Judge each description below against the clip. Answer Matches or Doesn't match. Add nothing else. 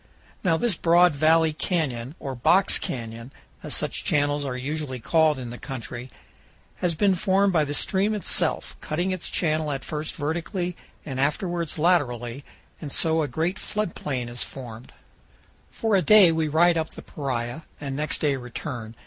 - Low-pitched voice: Doesn't match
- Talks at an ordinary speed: Matches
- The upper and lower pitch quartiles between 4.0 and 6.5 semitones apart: Matches